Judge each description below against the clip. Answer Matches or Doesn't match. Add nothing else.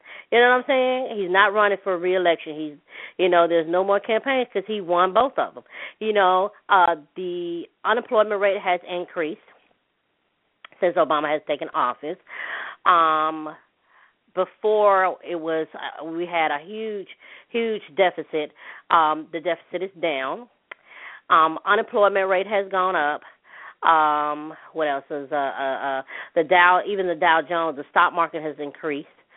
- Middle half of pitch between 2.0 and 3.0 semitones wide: Doesn't match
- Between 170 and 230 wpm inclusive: Doesn't match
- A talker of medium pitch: Matches